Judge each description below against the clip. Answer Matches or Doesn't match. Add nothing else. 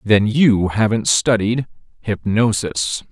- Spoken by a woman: Doesn't match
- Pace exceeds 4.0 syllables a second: Doesn't match